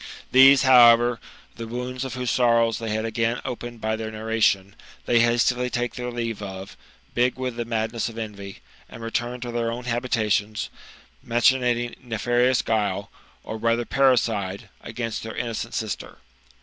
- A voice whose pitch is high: No, low, 115 Hz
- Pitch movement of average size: No, narrow, 1.8 semitones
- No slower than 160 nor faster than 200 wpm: No, average, 150 wpm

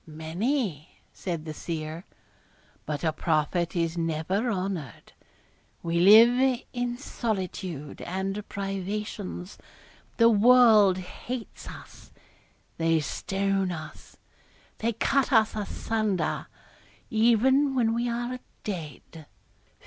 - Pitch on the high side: Yes, high, 195 Hz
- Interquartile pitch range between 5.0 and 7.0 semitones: Yes, wide, 5.6 semitones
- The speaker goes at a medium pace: No, slow, 95 wpm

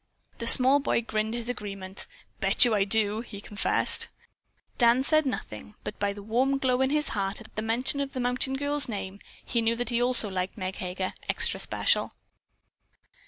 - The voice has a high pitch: Yes, high, 230 Hz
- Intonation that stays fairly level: No, average, 3.9 semitones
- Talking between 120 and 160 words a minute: No, average, 185 wpm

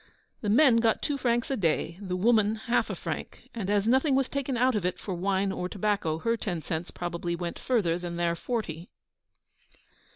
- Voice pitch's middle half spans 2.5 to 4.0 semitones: No, average, 5.3 semitones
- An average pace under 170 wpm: No, average, 195 wpm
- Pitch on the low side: No, high, 205 Hz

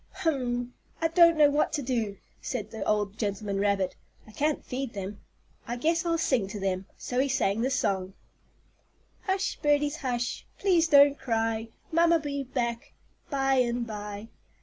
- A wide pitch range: Yes, wide, 5.7 semitones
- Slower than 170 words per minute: Yes, average, 160 wpm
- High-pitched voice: Yes, high, 245 Hz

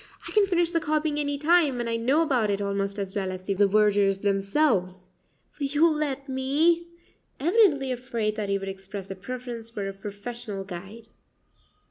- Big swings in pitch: Yes, wide, 6.7 semitones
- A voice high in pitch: Yes, high, 230 Hz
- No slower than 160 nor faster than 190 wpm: Yes, average, 175 wpm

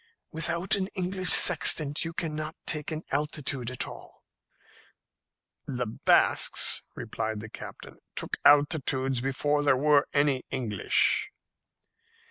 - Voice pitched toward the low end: No, medium, 145 Hz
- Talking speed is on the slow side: Yes, slow, 110 wpm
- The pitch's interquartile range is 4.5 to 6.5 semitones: No, average, 3.2 semitones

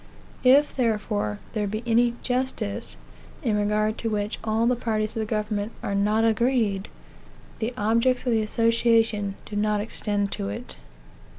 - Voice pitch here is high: Yes, high, 215 Hz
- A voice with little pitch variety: Yes, narrow, 2.0 semitones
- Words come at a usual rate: Yes, average, 155 wpm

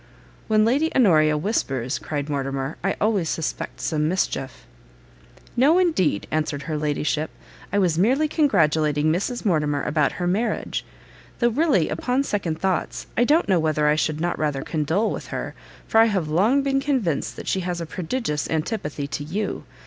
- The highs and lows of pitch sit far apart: Yes, wide, 6.8 semitones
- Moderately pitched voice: Yes, medium, 170 Hz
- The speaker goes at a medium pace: Yes, average, 165 wpm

